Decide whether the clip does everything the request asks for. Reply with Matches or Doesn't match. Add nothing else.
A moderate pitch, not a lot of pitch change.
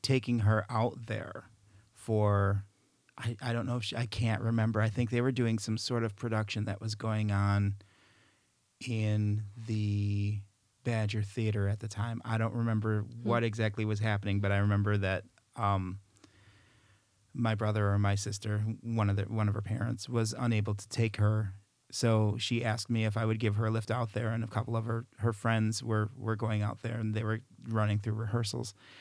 Doesn't match